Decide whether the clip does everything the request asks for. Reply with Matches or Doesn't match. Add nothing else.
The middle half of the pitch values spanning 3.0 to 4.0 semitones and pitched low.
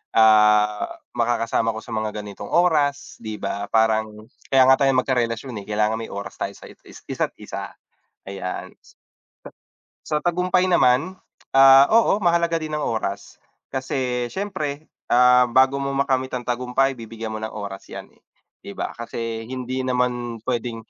Matches